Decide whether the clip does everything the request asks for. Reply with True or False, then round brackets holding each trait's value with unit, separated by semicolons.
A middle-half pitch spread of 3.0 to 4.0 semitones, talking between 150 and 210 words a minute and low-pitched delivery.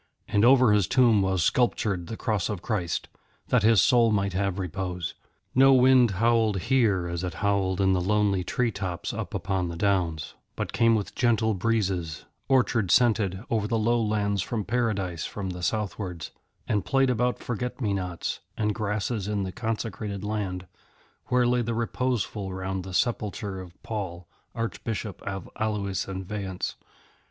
True (3.4 semitones; 160 wpm; 105 Hz)